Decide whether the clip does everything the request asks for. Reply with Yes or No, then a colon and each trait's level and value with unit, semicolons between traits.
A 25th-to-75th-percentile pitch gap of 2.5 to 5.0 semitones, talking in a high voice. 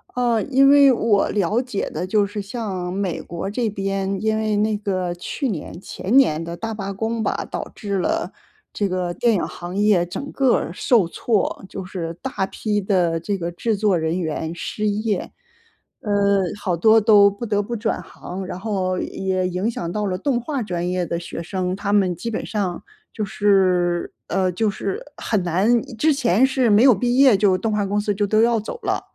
Yes: average, 3.3 semitones; high, 200 Hz